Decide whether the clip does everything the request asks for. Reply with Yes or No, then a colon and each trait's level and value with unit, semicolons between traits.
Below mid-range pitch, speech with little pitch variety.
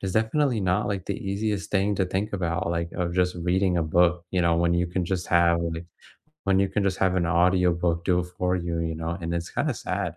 Yes: very low, 90 Hz; narrow, 2.0 semitones